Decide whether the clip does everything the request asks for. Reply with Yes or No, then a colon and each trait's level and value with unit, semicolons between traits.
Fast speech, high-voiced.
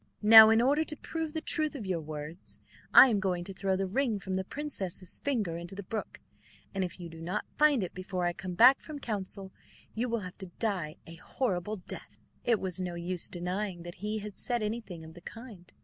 Yes: fast, 220 wpm; high, 195 Hz